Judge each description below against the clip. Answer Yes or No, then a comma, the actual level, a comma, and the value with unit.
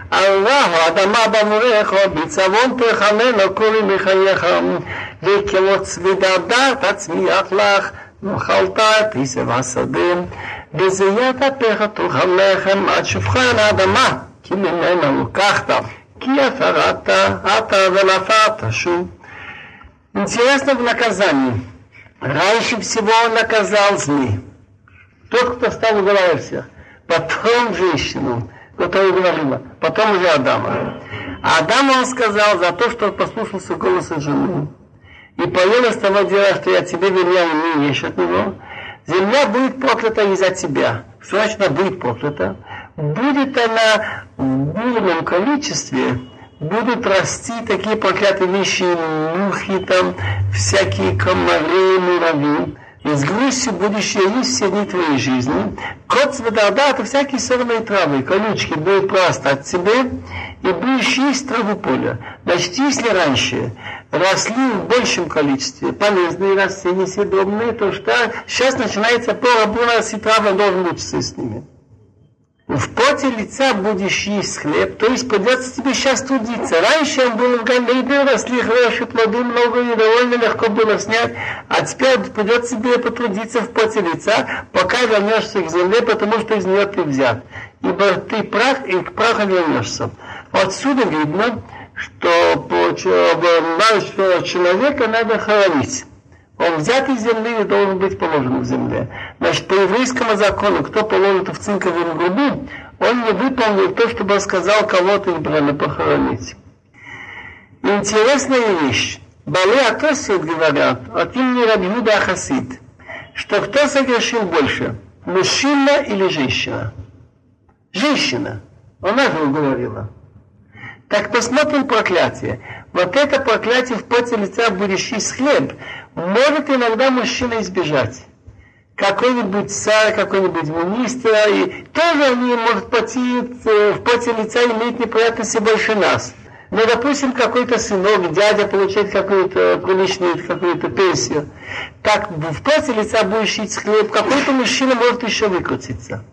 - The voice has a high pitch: Yes, high, 205 Hz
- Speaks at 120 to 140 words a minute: Yes, average, 130 wpm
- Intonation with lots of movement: No, average, 4.8 semitones